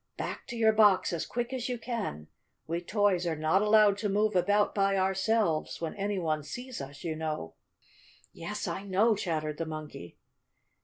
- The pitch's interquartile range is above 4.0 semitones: Yes, average, 5.1 semitones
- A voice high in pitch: Yes, high, 195 Hz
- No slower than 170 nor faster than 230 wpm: Yes, average, 175 wpm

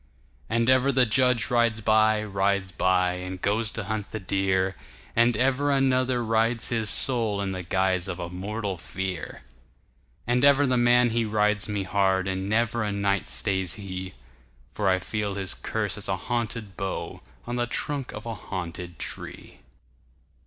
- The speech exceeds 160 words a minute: No, average, 145 wpm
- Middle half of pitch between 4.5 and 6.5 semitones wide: No, average, 3.8 semitones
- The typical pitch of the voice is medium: No, low, 105 Hz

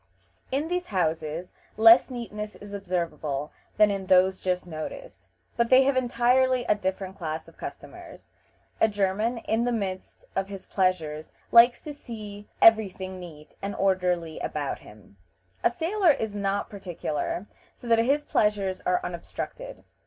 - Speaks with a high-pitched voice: Yes, high, 200 Hz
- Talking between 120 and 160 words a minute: Yes, average, 150 wpm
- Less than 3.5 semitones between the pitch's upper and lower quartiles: No, average, 4.6 semitones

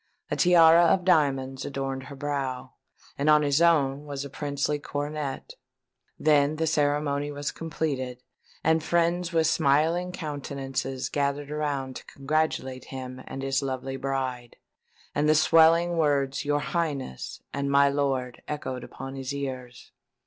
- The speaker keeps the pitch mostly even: Yes, narrow, 2.3 semitones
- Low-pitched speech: No, medium, 145 Hz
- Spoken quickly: No, average, 140 wpm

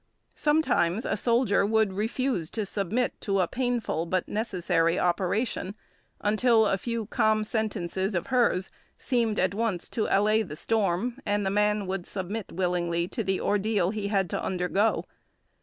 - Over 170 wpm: No, average, 155 wpm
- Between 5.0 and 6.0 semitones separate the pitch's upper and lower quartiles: No, average, 3.3 semitones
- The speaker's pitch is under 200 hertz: No, high, 205 Hz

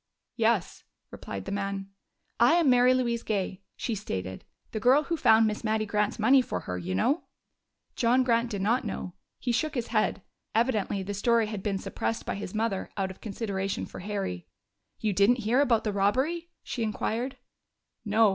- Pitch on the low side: No, high, 220 Hz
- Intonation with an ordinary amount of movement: Yes, average, 3.5 semitones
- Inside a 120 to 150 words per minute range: No, average, 180 wpm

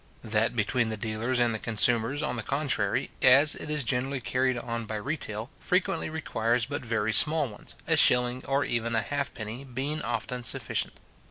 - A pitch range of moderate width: Yes, average, 3.7 semitones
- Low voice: Yes, low, 125 Hz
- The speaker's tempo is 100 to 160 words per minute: No, average, 175 wpm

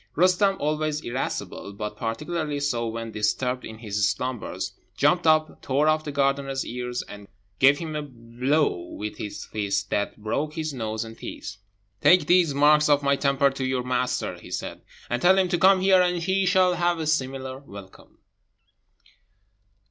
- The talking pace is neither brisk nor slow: Yes, average, 170 wpm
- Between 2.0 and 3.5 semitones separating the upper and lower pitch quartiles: No, average, 5.2 semitones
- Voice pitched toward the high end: No, medium, 140 Hz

